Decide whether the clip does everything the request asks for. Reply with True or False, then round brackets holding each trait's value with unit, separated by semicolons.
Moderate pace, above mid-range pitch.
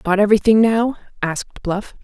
True (150 wpm; 205 Hz)